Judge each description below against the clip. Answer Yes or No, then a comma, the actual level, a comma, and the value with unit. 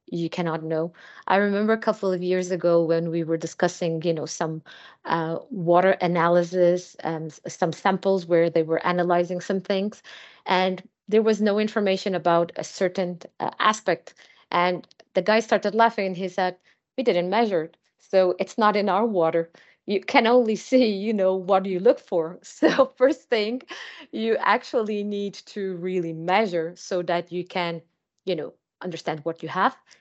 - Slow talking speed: No, average, 170 wpm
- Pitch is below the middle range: No, medium, 185 Hz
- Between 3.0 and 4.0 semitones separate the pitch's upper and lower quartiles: Yes, average, 3.3 semitones